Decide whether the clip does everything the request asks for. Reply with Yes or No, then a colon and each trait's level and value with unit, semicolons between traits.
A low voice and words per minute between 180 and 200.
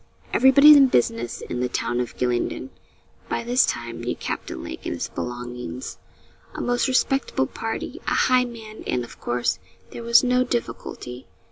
No: low, 130 Hz; average, 160 wpm